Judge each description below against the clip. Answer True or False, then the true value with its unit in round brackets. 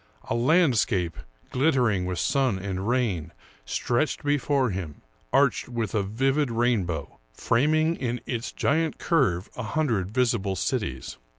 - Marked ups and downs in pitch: True (6.0 semitones)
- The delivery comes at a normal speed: False (125 wpm)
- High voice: False (120 Hz)